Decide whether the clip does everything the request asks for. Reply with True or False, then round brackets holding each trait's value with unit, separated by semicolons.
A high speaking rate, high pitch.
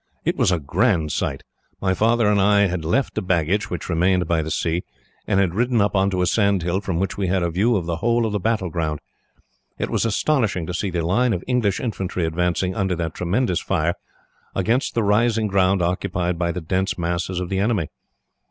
False (215 wpm; 95 Hz)